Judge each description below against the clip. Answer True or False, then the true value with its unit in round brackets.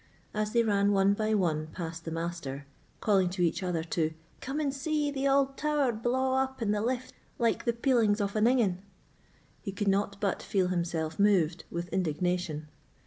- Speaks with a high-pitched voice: True (200 Hz)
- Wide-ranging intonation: True (5.7 semitones)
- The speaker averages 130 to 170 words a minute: False (185 wpm)